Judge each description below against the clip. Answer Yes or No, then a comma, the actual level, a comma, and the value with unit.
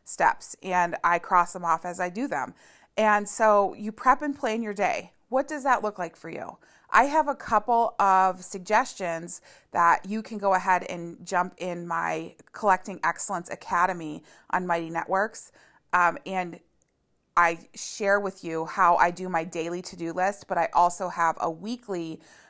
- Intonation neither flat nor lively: Yes, average, 3.6 semitones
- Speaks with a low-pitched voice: No, medium, 185 Hz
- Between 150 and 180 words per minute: Yes, average, 175 wpm